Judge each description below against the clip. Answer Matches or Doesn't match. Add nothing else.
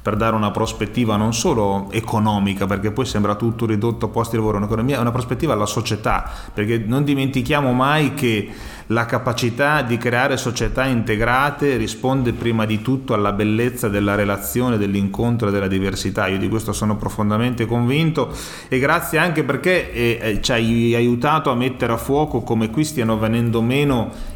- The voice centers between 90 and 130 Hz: Matches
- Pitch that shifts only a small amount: Doesn't match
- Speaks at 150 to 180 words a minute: Matches